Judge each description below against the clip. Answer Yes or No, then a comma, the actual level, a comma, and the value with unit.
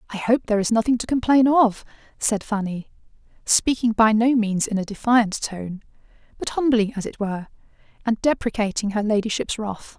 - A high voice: Yes, high, 220 Hz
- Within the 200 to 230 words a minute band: No, average, 170 wpm